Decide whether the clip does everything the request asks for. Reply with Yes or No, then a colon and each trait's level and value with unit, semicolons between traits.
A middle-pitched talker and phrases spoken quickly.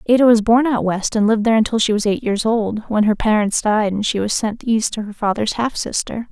No: high, 220 Hz; fast, 265 wpm